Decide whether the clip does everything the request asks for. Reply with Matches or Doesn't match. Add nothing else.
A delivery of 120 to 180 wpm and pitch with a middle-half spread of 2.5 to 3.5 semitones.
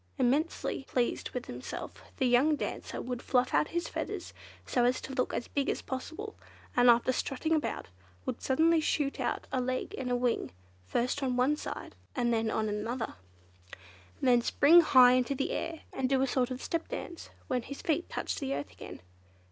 Doesn't match